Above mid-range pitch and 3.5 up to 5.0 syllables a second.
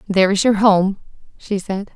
Yes: high, 195 Hz; 4.9 syllables/s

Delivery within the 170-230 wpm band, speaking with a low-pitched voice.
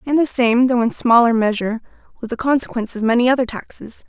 No: fast, 205 wpm; high, 240 Hz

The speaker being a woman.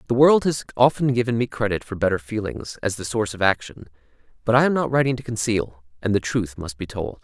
No: male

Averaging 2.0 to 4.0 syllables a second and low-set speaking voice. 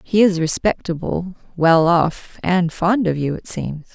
No: 3.9 syllables/s; medium, 175 Hz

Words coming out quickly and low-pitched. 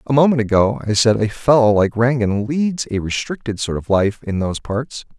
Yes: fast, 210 wpm; low, 115 Hz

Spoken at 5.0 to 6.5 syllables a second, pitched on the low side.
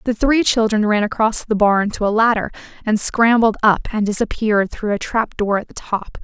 No: 5.1 syllables/s; high, 215 Hz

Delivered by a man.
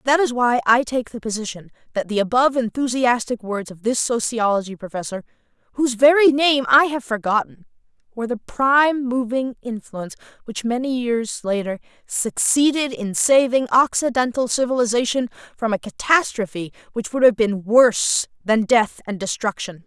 No: female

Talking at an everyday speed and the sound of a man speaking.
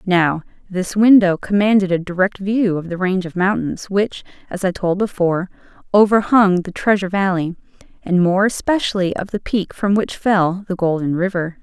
No: average, 170 wpm; female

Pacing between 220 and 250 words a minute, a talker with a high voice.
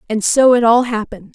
Yes: fast, 225 wpm; high, 230 Hz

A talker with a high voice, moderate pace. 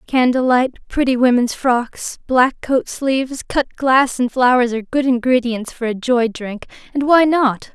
Yes: very high, 250 Hz; average, 170 wpm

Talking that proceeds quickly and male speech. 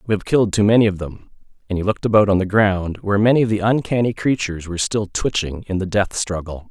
Yes: fast, 240 wpm; male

